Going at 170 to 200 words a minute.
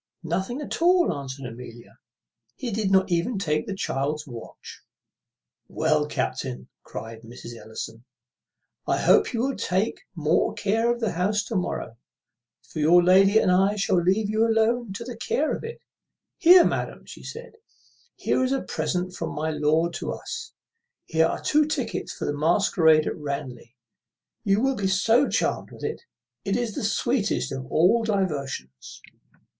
No: average, 160 wpm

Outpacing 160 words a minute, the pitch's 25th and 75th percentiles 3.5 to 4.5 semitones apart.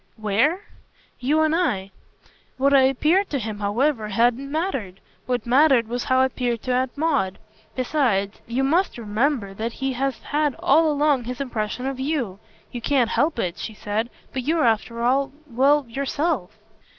Yes: average, 170 wpm; average, 4.0 semitones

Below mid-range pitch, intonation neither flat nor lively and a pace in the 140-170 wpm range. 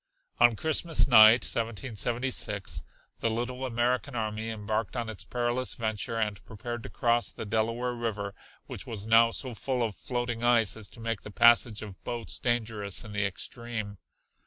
No: low, 115 Hz; narrow, 1.9 semitones; average, 160 wpm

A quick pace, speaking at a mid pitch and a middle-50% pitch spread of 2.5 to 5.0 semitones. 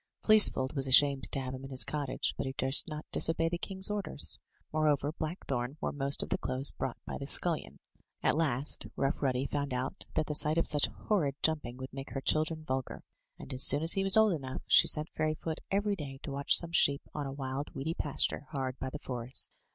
Yes: fast, 220 wpm; medium, 145 Hz; average, 3.0 semitones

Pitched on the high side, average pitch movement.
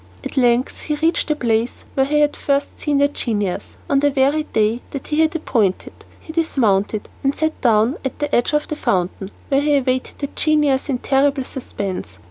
Yes: very high, 275 Hz; average, 4.1 semitones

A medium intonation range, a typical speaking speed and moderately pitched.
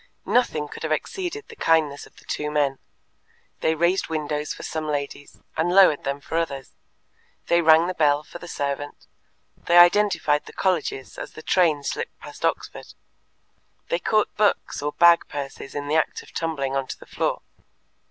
Yes: average, 3.2 semitones; average, 175 wpm; medium, 155 Hz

